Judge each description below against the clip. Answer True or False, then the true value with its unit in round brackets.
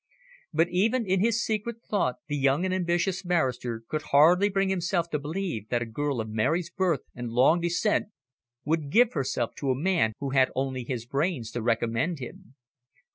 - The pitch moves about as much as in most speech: False (6.4 semitones)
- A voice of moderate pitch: True (155 Hz)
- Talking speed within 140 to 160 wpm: False (185 wpm)